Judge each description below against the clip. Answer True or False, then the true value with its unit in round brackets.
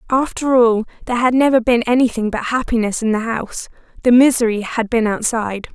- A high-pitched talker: True (235 Hz)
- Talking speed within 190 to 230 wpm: False (165 wpm)